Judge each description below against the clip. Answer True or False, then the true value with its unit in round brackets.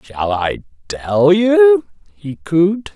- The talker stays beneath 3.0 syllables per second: True (2.7 syllables/s)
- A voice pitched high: False (165 Hz)